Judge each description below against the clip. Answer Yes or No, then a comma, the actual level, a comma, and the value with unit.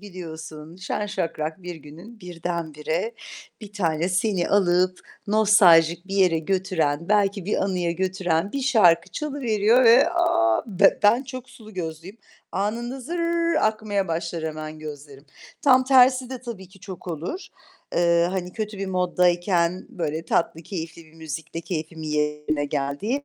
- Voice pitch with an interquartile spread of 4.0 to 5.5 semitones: Yes, average, 4.7 semitones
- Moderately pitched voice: Yes, medium, 180 Hz